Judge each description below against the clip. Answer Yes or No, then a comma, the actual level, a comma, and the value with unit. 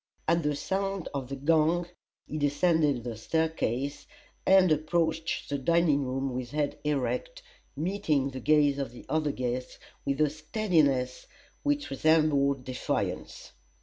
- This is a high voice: No, medium, 150 Hz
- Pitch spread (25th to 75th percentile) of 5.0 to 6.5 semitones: No, average, 3.2 semitones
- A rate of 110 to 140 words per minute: Yes, slow, 135 wpm